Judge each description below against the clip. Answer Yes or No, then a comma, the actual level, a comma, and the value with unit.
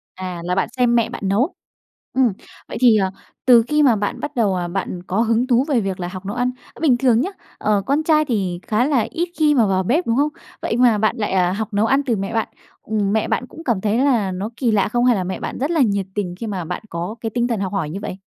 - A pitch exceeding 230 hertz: No, high, 220 Hz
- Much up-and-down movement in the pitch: No, average, 4.4 semitones